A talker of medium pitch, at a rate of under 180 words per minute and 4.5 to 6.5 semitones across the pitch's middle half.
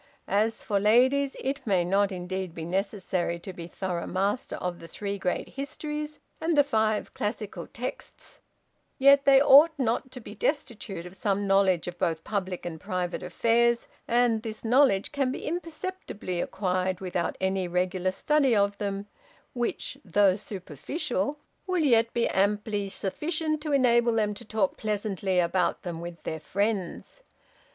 No: high, 205 Hz; average, 155 wpm; average, 5.2 semitones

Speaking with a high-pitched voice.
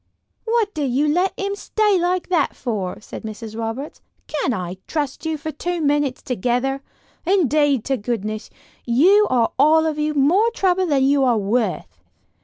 Yes: very high, 290 Hz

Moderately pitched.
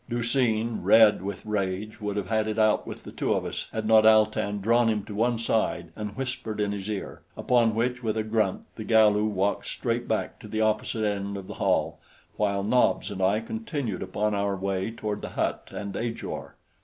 No: low, 110 Hz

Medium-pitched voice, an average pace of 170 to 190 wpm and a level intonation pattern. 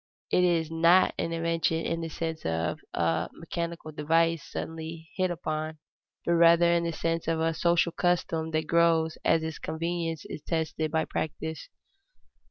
No: medium, 165 Hz; average, 160 wpm; narrow, 1.0 semitones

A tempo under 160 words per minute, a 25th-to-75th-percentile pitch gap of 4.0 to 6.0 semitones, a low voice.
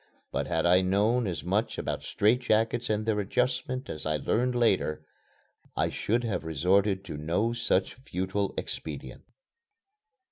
Yes: average, 145 wpm; average, 4.5 semitones; low, 105 Hz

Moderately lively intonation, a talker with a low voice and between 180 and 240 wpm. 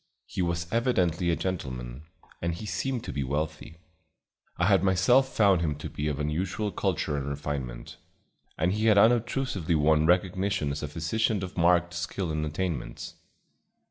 No: average, 4.4 semitones; very low, 85 Hz; average, 160 wpm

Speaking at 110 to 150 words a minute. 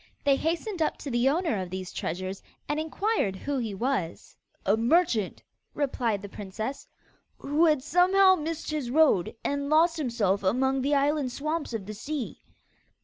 No: average, 160 wpm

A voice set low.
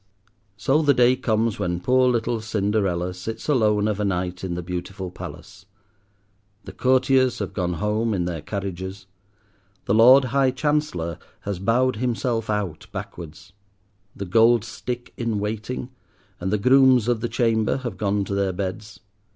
Yes: low, 110 Hz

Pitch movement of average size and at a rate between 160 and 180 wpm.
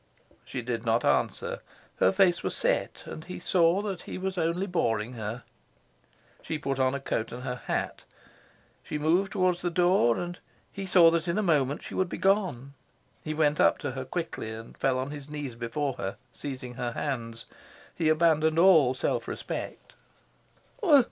No: wide, 5.8 semitones; average, 175 wpm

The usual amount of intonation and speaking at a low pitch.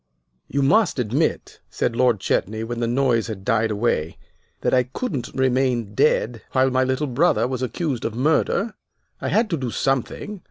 Yes: average, 3.1 semitones; low, 125 Hz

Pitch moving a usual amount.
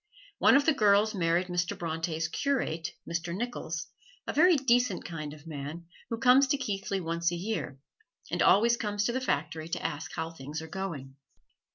No: wide, 6.0 semitones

